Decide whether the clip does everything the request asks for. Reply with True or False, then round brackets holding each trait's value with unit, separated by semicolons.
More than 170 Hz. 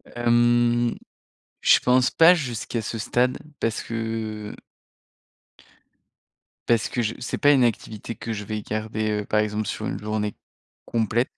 False (115 Hz)